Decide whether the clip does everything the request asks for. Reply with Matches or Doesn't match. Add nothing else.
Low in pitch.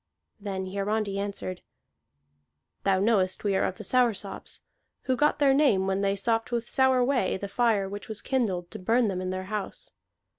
Doesn't match